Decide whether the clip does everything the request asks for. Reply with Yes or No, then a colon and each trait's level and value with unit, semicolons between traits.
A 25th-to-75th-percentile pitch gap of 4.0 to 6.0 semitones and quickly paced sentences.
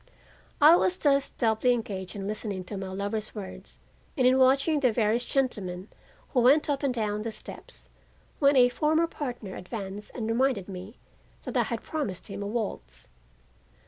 No: average, 5.0 semitones; average, 170 wpm